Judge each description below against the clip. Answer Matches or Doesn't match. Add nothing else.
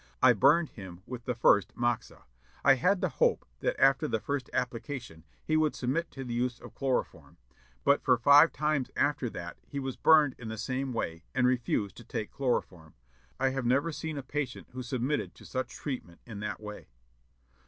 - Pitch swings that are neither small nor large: Matches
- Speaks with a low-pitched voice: Matches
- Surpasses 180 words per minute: Matches